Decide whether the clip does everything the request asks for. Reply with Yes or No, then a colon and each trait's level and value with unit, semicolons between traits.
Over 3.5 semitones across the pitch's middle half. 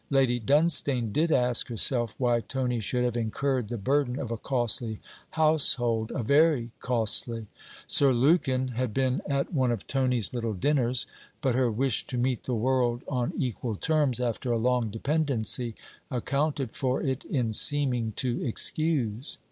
No: average, 2.7 semitones